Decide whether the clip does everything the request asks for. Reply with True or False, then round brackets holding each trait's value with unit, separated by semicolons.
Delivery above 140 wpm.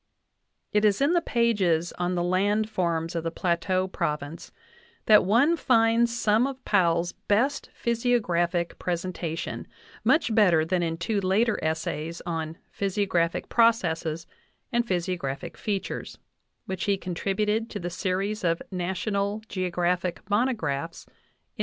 False (135 wpm)